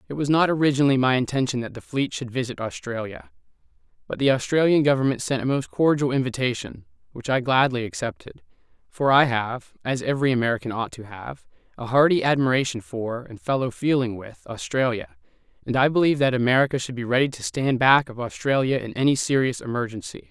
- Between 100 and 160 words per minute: No, average, 175 wpm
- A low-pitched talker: Yes, low, 130 Hz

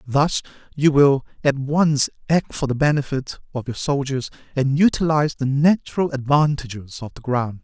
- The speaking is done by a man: Yes, male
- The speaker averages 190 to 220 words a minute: No, average, 155 wpm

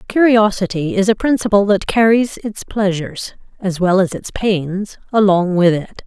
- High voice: Yes, high, 200 Hz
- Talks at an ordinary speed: Yes, average, 160 wpm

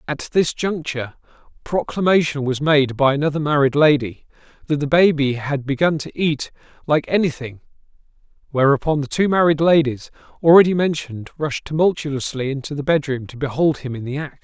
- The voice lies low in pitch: No, medium, 145 Hz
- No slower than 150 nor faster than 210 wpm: Yes, average, 155 wpm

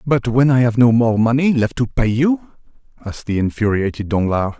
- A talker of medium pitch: No, low, 120 Hz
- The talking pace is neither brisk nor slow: Yes, average, 195 wpm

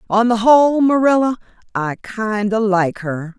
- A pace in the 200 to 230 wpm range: No, average, 160 wpm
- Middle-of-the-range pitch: No, high, 220 Hz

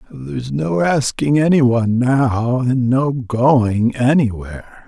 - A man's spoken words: Yes, male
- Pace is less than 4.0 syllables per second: Yes, 3.7 syllables/s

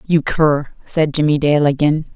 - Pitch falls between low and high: Yes, medium, 150 Hz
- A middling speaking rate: Yes, average, 165 wpm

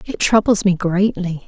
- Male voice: No, female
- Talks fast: No, average, 165 wpm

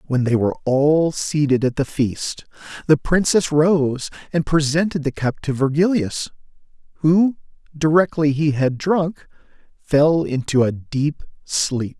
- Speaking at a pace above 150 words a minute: No, slow, 135 wpm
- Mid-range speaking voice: Yes, medium, 150 Hz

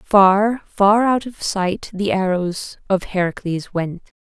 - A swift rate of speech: No, average, 140 wpm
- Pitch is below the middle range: No, high, 195 Hz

